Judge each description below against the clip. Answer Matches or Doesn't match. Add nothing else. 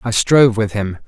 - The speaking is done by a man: Matches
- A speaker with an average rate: Doesn't match